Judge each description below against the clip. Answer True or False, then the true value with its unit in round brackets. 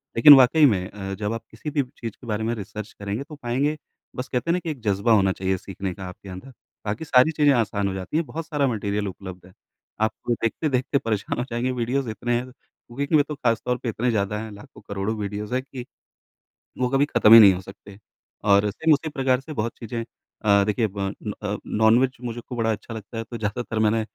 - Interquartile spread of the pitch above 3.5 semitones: True (3.9 semitones)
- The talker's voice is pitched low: True (115 Hz)